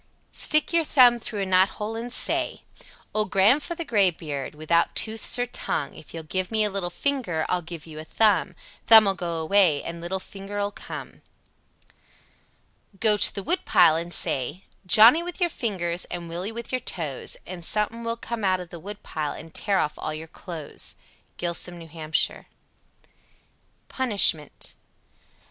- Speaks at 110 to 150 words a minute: No, average, 160 wpm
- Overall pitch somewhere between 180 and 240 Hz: Yes, high, 190 Hz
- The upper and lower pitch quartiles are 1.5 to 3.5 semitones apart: No, average, 4.8 semitones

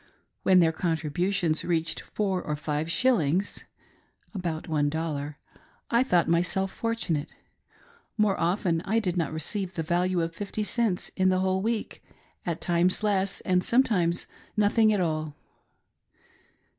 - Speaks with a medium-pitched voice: Yes, medium, 180 Hz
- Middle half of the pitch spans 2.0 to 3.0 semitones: No, average, 3.5 semitones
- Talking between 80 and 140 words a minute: Yes, slow, 135 wpm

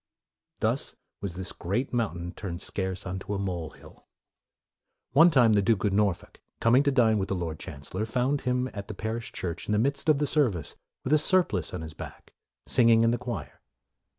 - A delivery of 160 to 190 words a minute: No, average, 200 wpm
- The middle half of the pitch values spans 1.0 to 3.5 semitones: No, average, 5.2 semitones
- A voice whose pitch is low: Yes, low, 105 Hz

